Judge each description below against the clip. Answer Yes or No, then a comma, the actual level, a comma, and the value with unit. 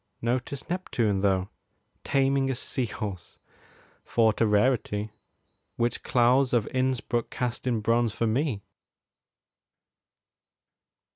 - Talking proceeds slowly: Yes, slow, 100 wpm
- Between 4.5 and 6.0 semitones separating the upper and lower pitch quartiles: No, average, 3.3 semitones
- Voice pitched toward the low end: Yes, low, 120 Hz